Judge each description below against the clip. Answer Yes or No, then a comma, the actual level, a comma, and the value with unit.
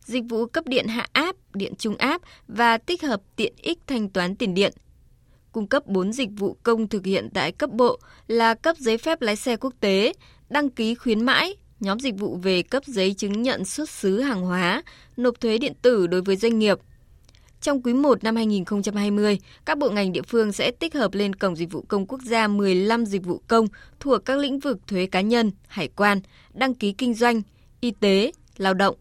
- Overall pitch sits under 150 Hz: No, high, 225 Hz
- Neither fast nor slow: Yes, average, 210 wpm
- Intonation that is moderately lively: Yes, average, 4.3 semitones